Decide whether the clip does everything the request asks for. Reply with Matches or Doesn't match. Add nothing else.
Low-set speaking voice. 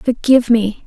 Doesn't match